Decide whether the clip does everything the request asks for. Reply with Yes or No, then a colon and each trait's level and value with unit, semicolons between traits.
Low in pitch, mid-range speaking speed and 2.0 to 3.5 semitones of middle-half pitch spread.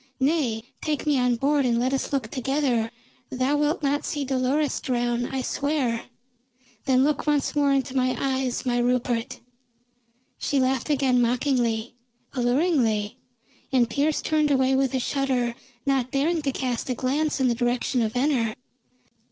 No: very high, 260 Hz; average, 155 wpm; average, 2.7 semitones